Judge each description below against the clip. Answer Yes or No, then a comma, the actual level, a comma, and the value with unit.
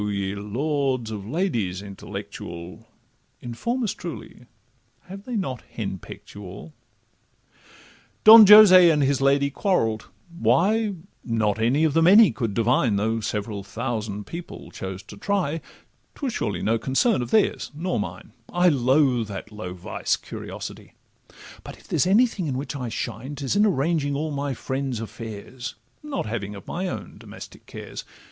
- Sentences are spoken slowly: No, average, 150 wpm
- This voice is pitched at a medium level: No, low, 130 Hz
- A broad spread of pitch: Yes, wide, 8.3 semitones